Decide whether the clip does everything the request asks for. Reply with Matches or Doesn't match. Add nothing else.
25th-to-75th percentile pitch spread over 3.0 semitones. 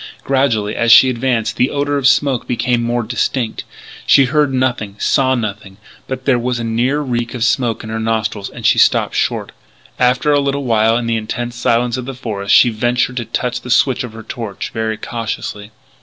Doesn't match